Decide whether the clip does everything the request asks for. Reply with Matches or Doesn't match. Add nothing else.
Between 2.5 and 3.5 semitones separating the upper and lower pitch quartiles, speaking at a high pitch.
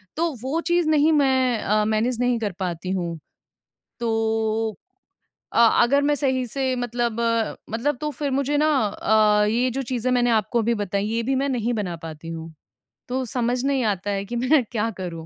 Doesn't match